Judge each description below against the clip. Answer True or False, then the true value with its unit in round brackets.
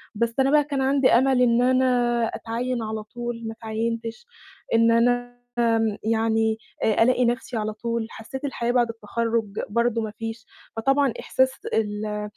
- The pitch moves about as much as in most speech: False (1.8 semitones)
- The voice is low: False (230 Hz)